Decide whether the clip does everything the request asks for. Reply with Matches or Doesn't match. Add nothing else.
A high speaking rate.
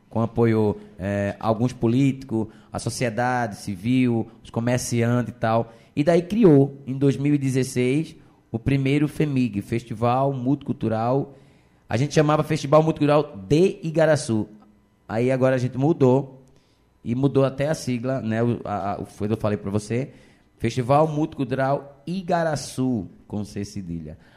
Doesn't match